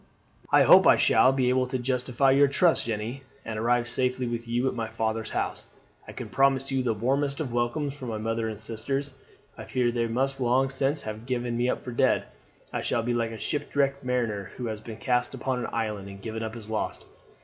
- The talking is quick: Yes, fast, 220 wpm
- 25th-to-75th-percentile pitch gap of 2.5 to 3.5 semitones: Yes, average, 2.9 semitones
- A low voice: Yes, low, 120 Hz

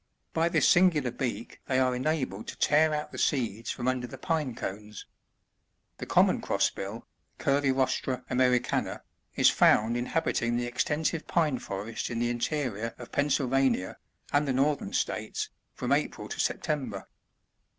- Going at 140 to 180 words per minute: Yes, average, 150 wpm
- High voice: No, low, 130 Hz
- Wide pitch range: No, average, 3.7 semitones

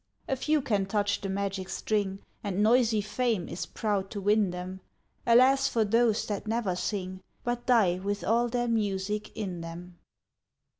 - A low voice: No, high, 205 Hz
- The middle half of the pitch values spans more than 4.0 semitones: No, average, 3.4 semitones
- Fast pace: No, average, 160 wpm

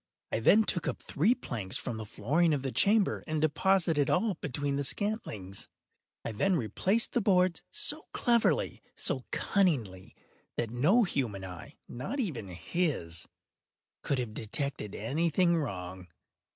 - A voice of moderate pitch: Yes, medium, 145 Hz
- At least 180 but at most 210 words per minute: No, average, 140 wpm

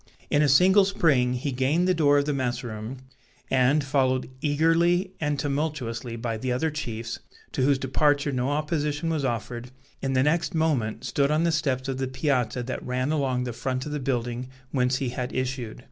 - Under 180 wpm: No, average, 190 wpm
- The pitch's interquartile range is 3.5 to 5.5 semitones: No, average, 3.1 semitones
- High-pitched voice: No, low, 135 Hz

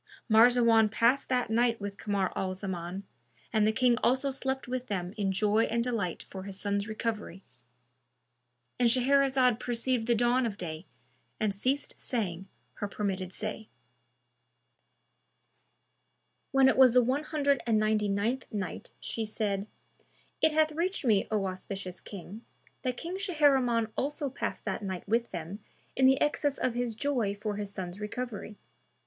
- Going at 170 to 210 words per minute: No, average, 150 wpm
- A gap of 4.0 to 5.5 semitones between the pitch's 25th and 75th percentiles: Yes, average, 4.4 semitones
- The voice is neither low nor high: No, high, 220 Hz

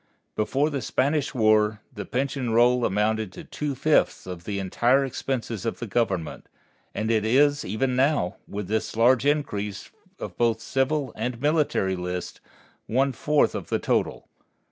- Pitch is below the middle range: Yes, low, 120 Hz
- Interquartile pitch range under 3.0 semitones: No, average, 4.3 semitones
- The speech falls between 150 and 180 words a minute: Yes, average, 160 wpm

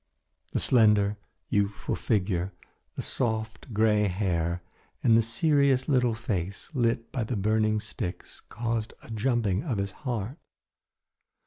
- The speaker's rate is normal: No, slow, 125 wpm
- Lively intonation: No, average, 2.9 semitones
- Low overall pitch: Yes, low, 110 Hz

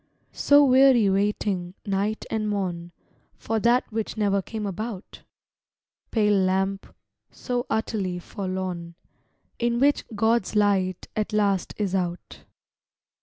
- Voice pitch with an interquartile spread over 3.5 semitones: No, average, 2.8 semitones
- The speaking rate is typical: No, slow, 115 wpm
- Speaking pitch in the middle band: No, high, 205 Hz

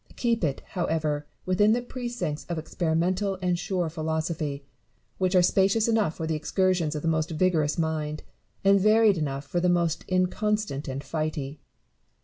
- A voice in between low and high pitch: Yes, medium, 170 Hz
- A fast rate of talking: No, average, 155 wpm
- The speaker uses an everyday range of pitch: Yes, average, 3.6 semitones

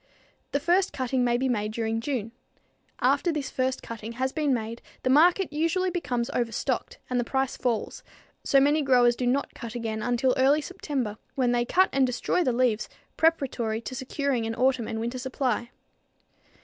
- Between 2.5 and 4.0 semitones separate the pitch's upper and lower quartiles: Yes, average, 3.1 semitones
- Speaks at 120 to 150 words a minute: No, average, 175 wpm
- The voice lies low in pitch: No, very high, 255 Hz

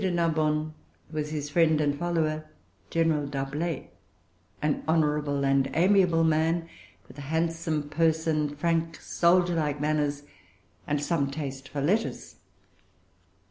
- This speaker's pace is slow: Yes, slow, 120 wpm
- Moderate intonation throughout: No, narrow, 2.1 semitones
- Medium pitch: Yes, medium, 155 Hz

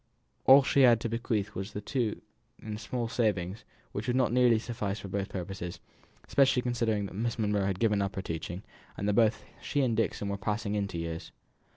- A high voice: No, low, 105 Hz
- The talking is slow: No, fast, 205 wpm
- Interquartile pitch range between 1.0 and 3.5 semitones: Yes, average, 3.1 semitones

